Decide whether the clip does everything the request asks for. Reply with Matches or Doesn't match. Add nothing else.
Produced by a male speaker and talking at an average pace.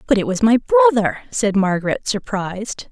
Doesn't match